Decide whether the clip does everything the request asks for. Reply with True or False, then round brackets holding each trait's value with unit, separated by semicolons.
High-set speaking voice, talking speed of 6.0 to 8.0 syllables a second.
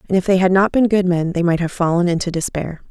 False (180 Hz; 6.3 syllables/s)